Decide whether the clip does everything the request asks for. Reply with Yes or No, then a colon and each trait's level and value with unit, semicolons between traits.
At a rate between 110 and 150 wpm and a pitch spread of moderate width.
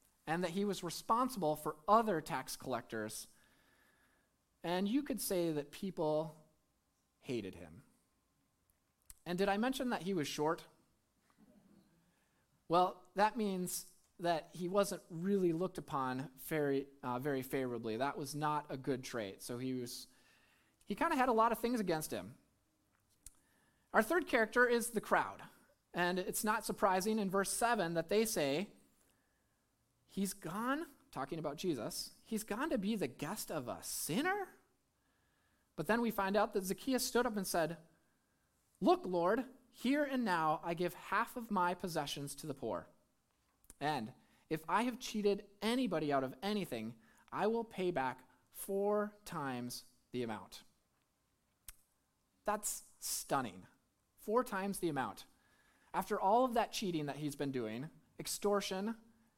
No: average, 145 wpm; wide, 6.5 semitones